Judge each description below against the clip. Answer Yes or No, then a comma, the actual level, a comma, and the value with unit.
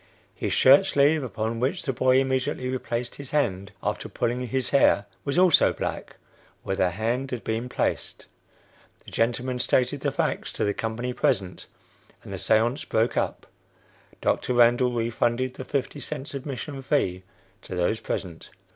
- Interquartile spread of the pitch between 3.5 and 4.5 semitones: No, average, 3.1 semitones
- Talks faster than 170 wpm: No, average, 155 wpm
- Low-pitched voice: Yes, low, 125 Hz